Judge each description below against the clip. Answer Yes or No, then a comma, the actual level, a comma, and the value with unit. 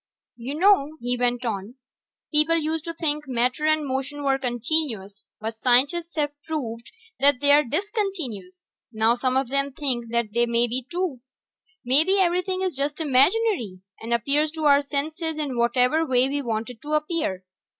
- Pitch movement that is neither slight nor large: Yes, average, 4.5 semitones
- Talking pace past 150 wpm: Yes, average, 165 wpm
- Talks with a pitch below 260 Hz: No, very high, 275 Hz